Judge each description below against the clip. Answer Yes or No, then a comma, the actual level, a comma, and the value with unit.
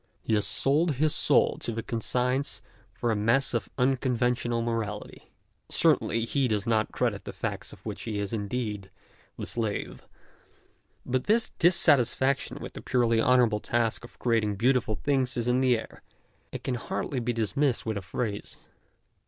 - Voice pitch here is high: No, low, 120 Hz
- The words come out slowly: No, average, 160 wpm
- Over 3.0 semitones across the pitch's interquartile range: No, average, 2.7 semitones